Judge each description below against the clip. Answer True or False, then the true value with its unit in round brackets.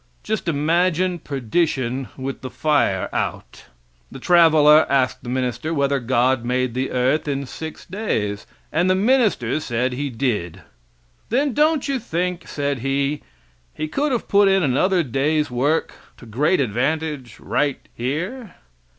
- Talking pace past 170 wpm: False (140 wpm)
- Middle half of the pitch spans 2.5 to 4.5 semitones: False (5.4 semitones)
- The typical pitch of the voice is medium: True (145 Hz)